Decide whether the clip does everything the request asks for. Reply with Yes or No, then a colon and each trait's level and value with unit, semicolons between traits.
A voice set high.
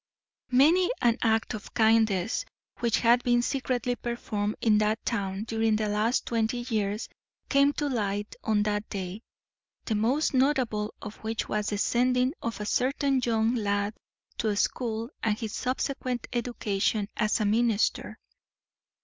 Yes: high, 225 Hz